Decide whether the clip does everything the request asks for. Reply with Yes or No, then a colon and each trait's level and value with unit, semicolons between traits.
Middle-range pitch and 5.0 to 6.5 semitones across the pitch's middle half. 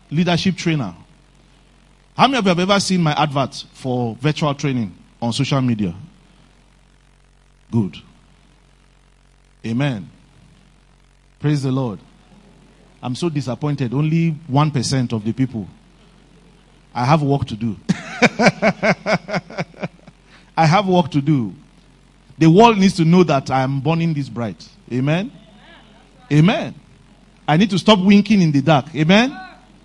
Yes: medium, 155 Hz; wide, 5.6 semitones